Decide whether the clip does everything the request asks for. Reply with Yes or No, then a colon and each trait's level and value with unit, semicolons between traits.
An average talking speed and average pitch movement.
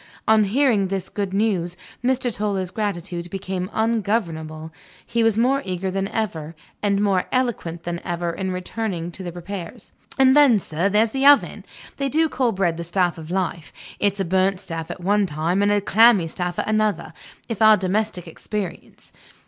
Yes: average, 175 wpm; average, 3.9 semitones